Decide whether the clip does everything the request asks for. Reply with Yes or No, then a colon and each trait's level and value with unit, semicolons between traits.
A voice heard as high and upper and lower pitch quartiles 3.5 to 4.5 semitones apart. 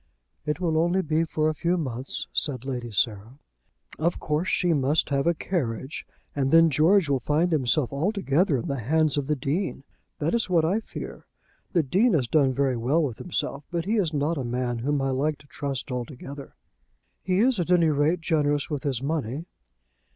No: medium, 150 Hz; average, 3.8 semitones